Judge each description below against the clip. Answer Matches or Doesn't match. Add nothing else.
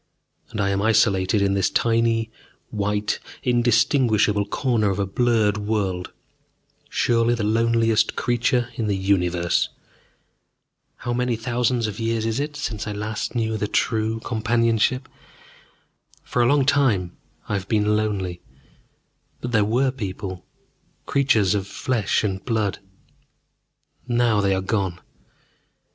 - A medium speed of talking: Doesn't match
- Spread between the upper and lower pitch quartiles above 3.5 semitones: Doesn't match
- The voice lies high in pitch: Doesn't match